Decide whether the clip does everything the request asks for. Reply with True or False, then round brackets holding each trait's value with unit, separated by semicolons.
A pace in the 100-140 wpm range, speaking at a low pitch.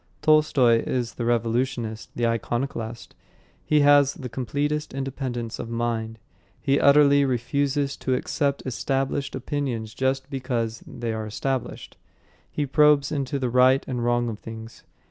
True (135 wpm; 130 Hz)